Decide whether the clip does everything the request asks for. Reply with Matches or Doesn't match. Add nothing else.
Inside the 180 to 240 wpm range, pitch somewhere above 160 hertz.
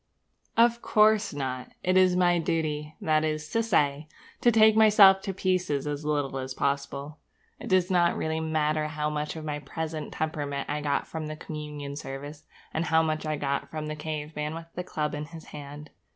Doesn't match